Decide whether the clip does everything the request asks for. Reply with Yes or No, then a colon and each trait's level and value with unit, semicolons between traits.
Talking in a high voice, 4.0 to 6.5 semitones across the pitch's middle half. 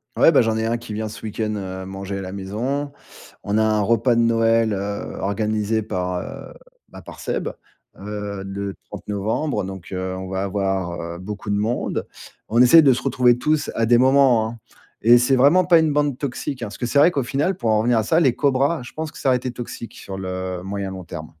No: low, 110 Hz; average, 4.3 semitones